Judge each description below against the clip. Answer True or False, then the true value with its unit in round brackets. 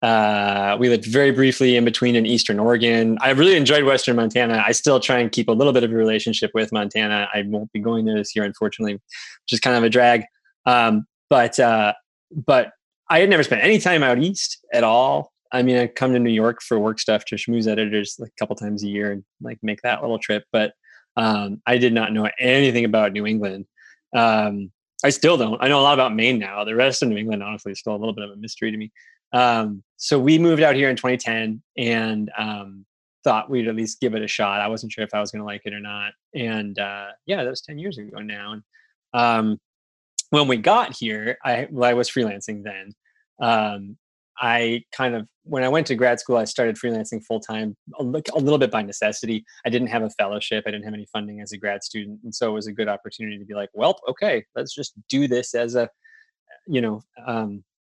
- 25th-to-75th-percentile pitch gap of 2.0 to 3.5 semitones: True (2.7 semitones)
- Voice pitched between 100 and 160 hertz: True (115 Hz)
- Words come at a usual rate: False (230 wpm)